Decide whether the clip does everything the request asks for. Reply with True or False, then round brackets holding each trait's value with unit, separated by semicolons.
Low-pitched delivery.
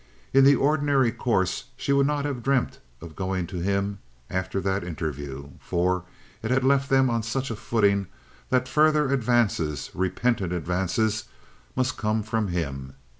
True (110 Hz)